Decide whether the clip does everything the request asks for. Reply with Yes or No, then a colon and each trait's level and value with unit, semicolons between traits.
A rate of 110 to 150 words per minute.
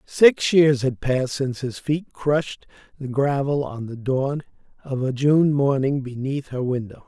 No: average, 170 wpm